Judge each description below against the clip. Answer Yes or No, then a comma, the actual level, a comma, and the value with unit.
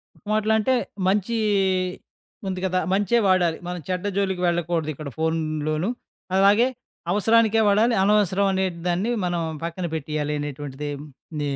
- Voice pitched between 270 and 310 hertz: No, medium, 185 Hz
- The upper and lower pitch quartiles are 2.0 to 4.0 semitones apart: No, average, 4.5 semitones